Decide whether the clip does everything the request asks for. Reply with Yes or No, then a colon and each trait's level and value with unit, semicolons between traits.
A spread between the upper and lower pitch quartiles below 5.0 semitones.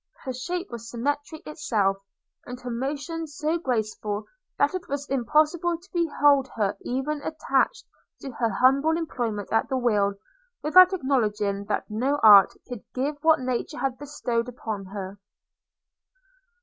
No: average, 5.3 semitones